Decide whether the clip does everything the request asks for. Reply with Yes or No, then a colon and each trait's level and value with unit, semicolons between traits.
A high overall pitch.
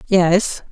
No: medium, 180 Hz